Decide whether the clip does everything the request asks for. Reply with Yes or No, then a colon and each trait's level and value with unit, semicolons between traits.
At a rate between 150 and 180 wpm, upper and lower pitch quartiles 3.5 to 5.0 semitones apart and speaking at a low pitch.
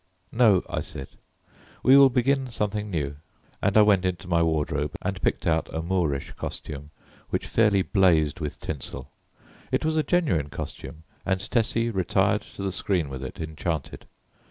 No: average, 160 wpm; wide, 5.6 semitones; very low, 90 Hz